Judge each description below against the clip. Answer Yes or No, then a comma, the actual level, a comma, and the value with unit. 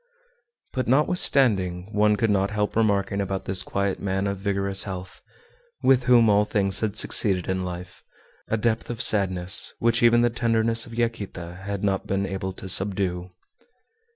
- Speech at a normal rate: Yes, average, 160 wpm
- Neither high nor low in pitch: No, low, 100 Hz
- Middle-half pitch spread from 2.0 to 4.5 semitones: Yes, average, 3.1 semitones